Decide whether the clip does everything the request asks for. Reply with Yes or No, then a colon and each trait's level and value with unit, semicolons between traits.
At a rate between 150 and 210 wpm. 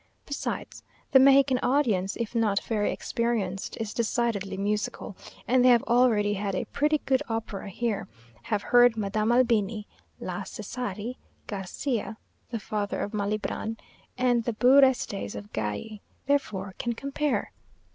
No: slow, 135 wpm